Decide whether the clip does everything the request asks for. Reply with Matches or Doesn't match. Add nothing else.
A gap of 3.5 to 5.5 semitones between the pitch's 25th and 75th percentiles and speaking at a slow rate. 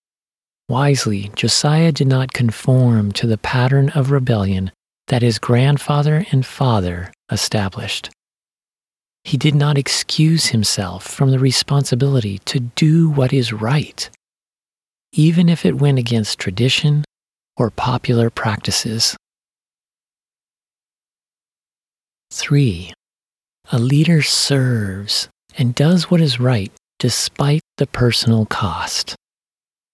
Matches